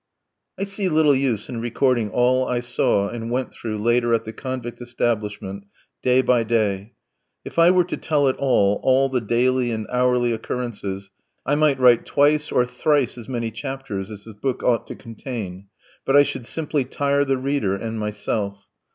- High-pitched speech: No, low, 120 Hz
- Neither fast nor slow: Yes, average, 180 wpm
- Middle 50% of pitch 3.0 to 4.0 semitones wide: Yes, average, 3.4 semitones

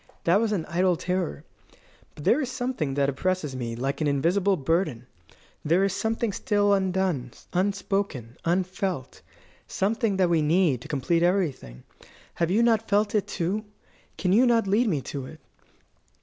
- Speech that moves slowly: No, average, 160 wpm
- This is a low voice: No, medium, 185 Hz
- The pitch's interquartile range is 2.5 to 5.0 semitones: No, wide, 5.4 semitones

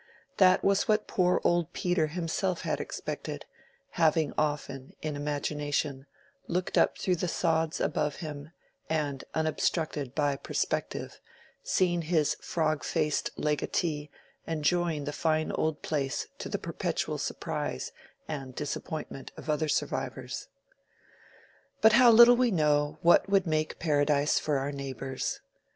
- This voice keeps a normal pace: No, slow, 130 wpm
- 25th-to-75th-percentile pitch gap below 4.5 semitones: Yes, average, 2.9 semitones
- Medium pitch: Yes, medium, 155 Hz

